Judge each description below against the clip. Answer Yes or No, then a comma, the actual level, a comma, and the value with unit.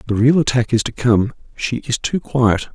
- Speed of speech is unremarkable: Yes, average, 195 wpm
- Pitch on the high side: No, low, 125 Hz